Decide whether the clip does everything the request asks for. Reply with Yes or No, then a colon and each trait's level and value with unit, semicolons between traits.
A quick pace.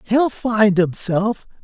No: slow, 110 wpm